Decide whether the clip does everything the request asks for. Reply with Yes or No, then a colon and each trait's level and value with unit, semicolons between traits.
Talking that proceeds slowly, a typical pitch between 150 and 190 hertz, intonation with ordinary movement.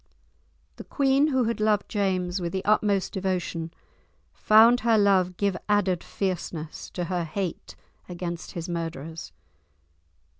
Yes: slow, 125 wpm; medium, 185 Hz; average, 3.4 semitones